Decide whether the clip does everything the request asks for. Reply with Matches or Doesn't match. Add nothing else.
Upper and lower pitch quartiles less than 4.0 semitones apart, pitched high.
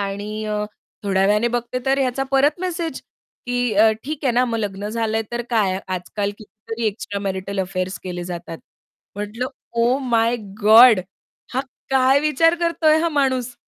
Doesn't match